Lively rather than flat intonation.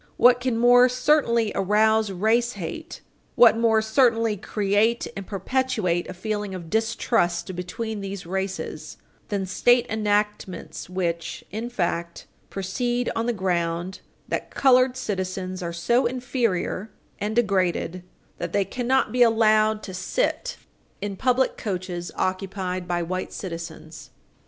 No: average, 4.2 semitones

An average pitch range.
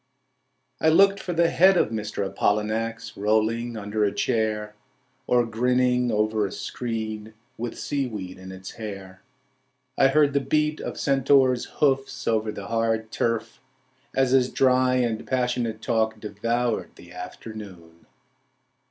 Yes: average, 3.1 semitones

